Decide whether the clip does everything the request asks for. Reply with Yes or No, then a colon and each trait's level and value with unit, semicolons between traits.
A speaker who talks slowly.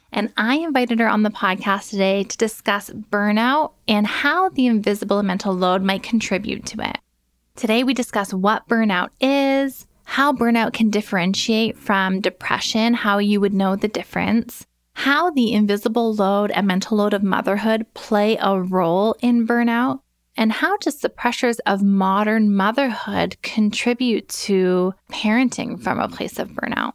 No: average, 155 wpm